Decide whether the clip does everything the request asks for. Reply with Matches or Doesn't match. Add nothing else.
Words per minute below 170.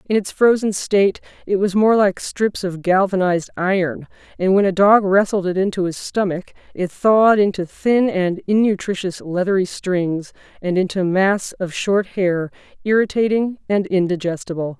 Matches